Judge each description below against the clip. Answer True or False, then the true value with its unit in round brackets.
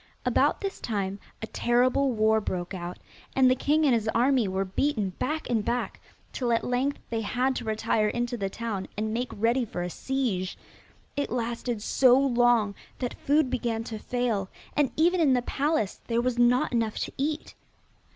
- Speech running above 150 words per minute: True (180 wpm)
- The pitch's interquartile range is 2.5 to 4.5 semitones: True (3.2 semitones)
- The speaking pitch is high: True (240 Hz)